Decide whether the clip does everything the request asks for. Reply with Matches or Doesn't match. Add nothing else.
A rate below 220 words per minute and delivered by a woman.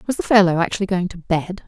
Doesn't match